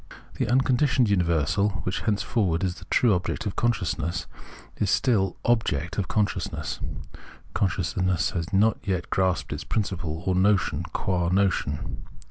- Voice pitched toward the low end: Yes, very low, 95 Hz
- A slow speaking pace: Yes, slow, 130 wpm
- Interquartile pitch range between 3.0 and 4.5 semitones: Yes, average, 3.4 semitones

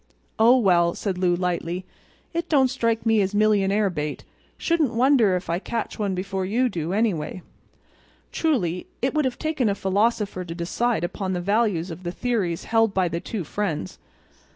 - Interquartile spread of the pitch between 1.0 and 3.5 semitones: No, average, 4.6 semitones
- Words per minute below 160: No, average, 175 wpm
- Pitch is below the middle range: No, high, 200 Hz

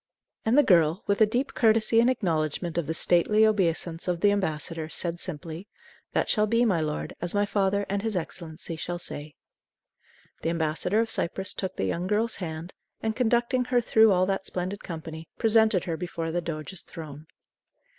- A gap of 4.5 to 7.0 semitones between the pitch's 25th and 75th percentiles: Yes, average, 4.8 semitones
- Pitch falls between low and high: Yes, medium, 180 Hz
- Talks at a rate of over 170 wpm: Yes, average, 180 wpm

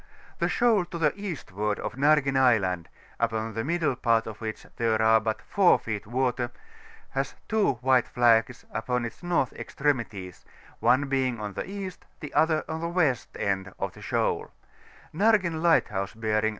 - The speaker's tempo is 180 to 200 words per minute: No, average, 165 wpm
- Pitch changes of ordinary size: No, wide, 6.3 semitones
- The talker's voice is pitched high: No, low, 125 Hz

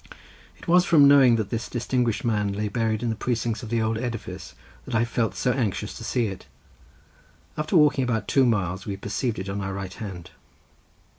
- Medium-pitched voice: No, low, 115 Hz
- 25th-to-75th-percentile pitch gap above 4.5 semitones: No, average, 3.3 semitones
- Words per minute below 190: No, average, 200 wpm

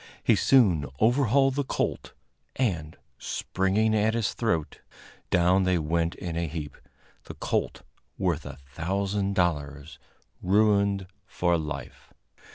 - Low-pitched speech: Yes, very low, 95 Hz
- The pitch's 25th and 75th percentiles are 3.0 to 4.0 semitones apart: No, average, 4.5 semitones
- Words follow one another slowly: Yes, slow, 120 wpm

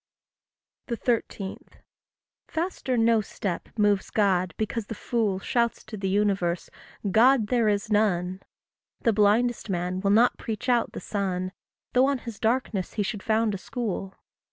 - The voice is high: Yes, high, 210 Hz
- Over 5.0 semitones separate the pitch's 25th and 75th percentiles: No, average, 3.2 semitones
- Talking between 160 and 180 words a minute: No, average, 145 wpm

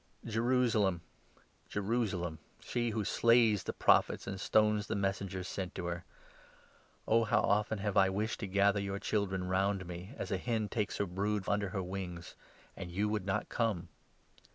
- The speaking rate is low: No, average, 195 wpm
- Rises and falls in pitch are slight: Yes, narrow, 2.3 semitones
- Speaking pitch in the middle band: No, low, 100 Hz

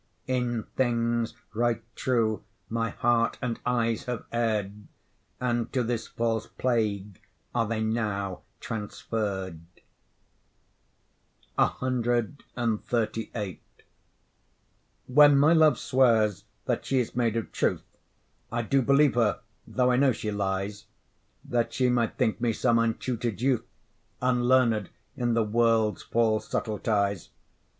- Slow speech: Yes, slow, 115 wpm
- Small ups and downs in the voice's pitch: Yes, narrow, 2.3 semitones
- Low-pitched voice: Yes, low, 115 Hz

